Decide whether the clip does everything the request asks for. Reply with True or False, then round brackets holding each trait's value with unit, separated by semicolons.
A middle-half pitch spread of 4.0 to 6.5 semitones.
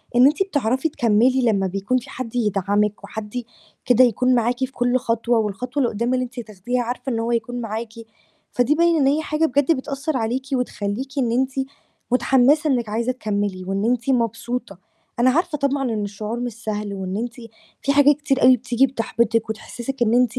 False (3.2 semitones)